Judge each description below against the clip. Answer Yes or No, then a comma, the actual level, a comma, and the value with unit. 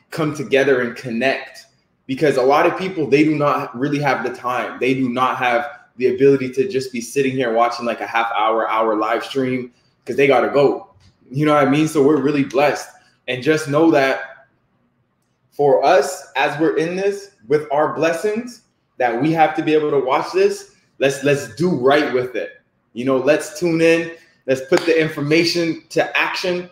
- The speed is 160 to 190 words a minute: No, average, 200 wpm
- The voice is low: No, medium, 145 Hz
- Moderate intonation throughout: Yes, average, 3.9 semitones